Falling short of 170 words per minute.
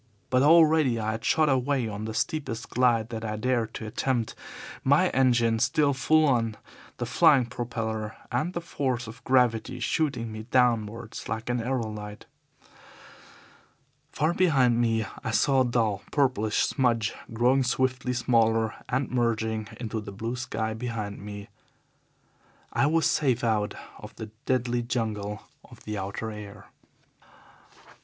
Yes: average, 140 wpm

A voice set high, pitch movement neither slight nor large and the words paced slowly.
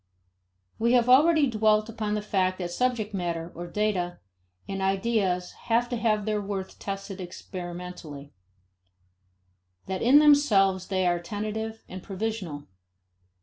Yes: high, 200 Hz; average, 3.6 semitones; slow, 130 wpm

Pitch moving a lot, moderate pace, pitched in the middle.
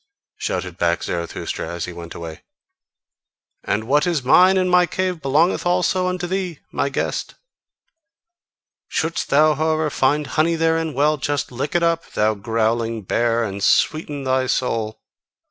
Yes: wide, 6.7 semitones; average, 145 wpm; medium, 145 Hz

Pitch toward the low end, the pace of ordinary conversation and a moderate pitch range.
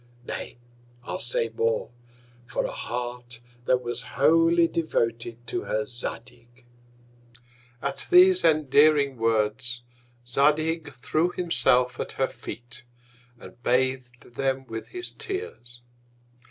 No: low, 125 Hz; slow, 110 wpm; average, 4.2 semitones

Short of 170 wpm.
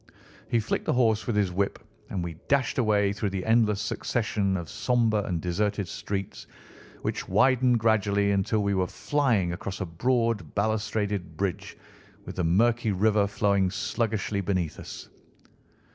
Yes: average, 150 wpm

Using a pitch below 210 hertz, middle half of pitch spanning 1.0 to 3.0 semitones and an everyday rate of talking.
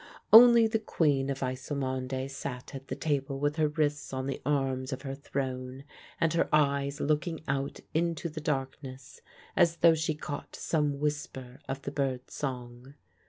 Yes: medium, 140 Hz; narrow, 2.4 semitones; average, 165 wpm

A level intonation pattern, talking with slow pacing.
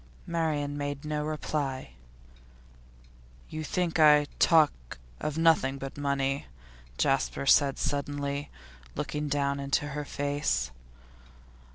Yes: narrow, 1.4 semitones; slow, 100 wpm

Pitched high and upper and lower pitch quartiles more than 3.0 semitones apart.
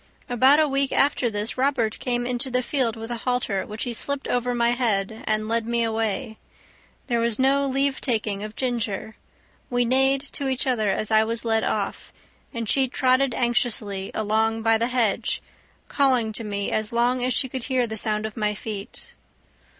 No: high, 235 Hz; average, 2.7 semitones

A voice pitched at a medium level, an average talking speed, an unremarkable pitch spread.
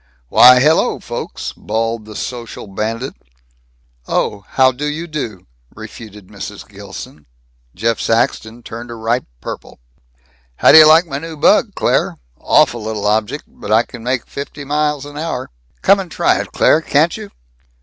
No: low, 120 Hz; average, 155 wpm; average, 5.0 semitones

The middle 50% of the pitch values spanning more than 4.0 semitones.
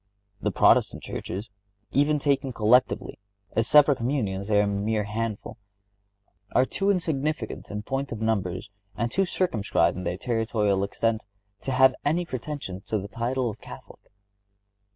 Yes: average, 4.9 semitones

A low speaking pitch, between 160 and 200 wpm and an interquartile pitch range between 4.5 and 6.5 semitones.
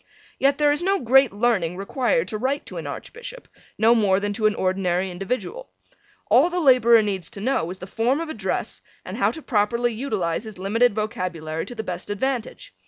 No: high, 220 Hz; average, 195 wpm; wide, 5.6 semitones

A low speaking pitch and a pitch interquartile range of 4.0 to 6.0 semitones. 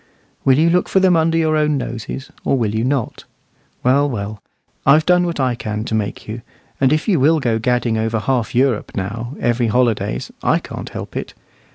Yes: low, 125 Hz; average, 5.2 semitones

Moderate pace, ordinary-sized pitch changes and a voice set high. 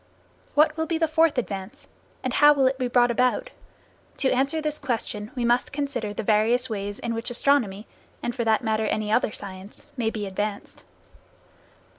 Yes: average, 180 wpm; average, 4.5 semitones; high, 240 Hz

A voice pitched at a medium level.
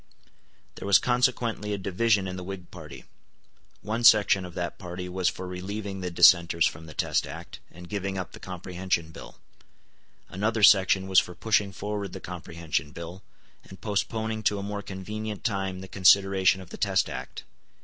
No: very low, 95 Hz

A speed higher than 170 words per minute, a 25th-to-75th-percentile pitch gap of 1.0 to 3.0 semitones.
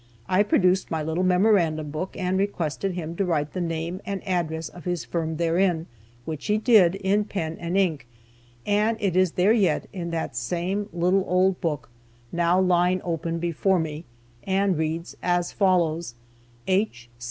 No: average, 165 wpm; average, 2.7 semitones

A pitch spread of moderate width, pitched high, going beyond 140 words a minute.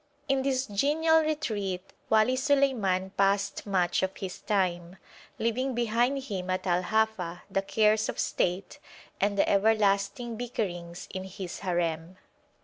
No: average, 4.4 semitones; high, 200 Hz; slow, 135 wpm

